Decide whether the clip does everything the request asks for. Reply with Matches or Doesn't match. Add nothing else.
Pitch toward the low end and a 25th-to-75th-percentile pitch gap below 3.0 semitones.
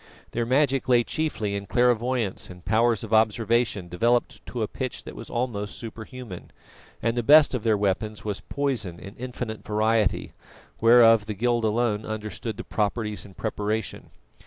Matches